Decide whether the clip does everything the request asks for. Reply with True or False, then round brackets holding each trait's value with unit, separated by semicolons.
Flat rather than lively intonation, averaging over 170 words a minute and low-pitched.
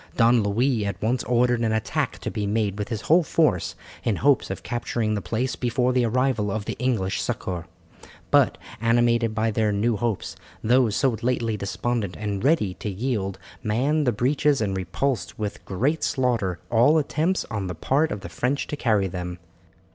False (3.7 semitones; 180 wpm; 115 Hz)